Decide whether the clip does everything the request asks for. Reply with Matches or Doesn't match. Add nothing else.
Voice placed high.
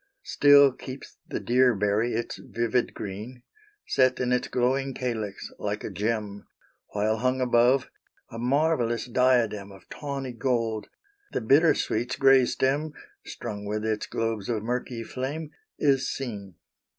Doesn't match